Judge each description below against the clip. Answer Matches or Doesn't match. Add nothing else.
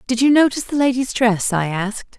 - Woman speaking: Matches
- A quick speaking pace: Matches